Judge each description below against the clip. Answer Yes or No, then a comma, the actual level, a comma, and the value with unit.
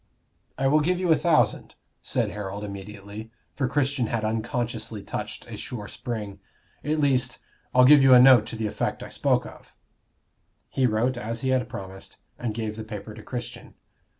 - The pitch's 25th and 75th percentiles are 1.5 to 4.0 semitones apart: Yes, average, 3.5 semitones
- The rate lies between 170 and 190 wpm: Yes, average, 180 wpm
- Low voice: Yes, low, 115 Hz